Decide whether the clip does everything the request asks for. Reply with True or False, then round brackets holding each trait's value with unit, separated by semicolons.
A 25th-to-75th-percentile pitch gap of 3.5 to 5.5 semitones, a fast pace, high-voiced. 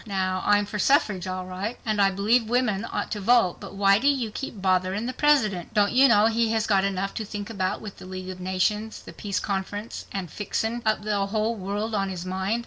False (2.8 semitones; 225 wpm; 205 Hz)